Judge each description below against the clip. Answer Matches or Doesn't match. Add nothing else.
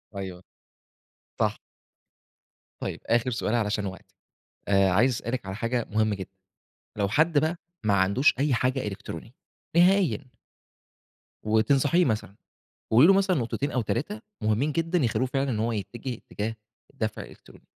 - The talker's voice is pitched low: Matches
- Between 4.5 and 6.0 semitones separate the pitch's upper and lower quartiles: Matches